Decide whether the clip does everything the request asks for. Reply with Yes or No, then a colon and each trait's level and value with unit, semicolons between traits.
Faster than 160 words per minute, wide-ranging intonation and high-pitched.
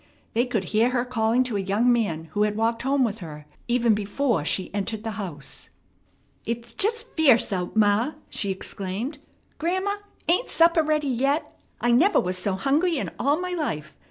Yes: average, 180 wpm; wide, 5.7 semitones; high, 235 Hz